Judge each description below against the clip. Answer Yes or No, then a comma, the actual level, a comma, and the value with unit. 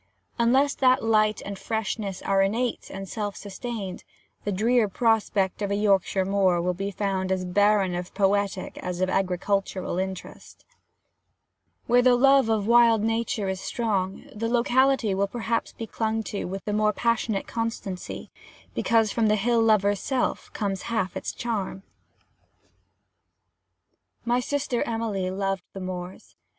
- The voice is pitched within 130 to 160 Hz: No, high, 205 Hz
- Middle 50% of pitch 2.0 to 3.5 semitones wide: Yes, average, 3.0 semitones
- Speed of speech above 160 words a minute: No, average, 145 wpm